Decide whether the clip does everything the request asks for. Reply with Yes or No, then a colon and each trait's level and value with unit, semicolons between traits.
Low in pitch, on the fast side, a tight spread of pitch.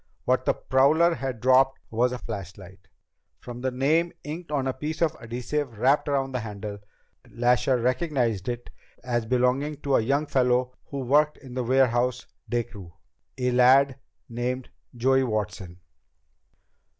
No: low, 125 Hz; average, 150 wpm; narrow, 2.3 semitones